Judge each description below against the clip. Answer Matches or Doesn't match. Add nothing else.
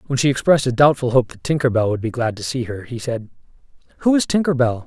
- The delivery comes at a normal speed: Doesn't match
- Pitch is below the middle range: Matches